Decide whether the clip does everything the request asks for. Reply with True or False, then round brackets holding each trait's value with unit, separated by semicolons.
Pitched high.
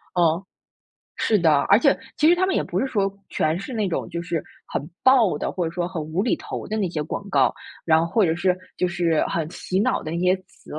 False (180 Hz)